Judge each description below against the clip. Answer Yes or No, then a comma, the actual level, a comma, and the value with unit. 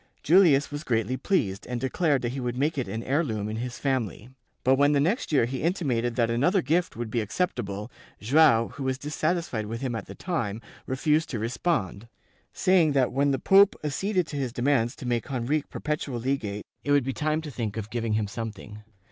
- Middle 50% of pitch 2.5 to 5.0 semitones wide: Yes, average, 4.7 semitones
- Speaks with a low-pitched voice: Yes, low, 130 Hz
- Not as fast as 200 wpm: No, fast, 205 wpm